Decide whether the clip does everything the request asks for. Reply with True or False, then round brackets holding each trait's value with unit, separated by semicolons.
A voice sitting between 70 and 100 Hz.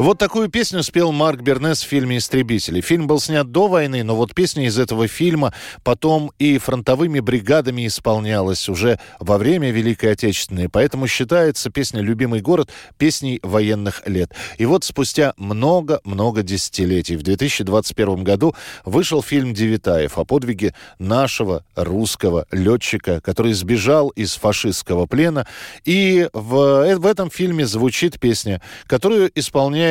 False (125 Hz)